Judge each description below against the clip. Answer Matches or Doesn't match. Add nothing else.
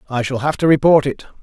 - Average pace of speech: Doesn't match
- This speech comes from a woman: Doesn't match